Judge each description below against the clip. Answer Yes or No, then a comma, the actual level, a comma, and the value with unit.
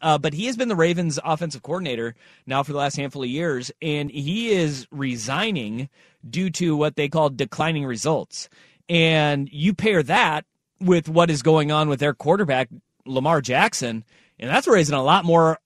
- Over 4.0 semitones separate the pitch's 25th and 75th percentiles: No, average, 3.7 semitones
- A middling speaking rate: Yes, average, 180 wpm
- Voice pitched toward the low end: No, medium, 155 Hz